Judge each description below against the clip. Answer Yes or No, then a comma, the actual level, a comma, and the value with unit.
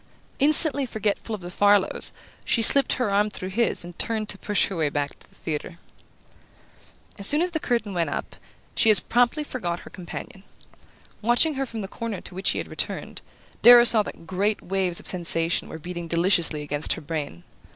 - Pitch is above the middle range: Yes, high, 200 Hz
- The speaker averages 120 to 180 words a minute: No, average, 195 wpm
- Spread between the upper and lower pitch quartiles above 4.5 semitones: Yes, average, 5.1 semitones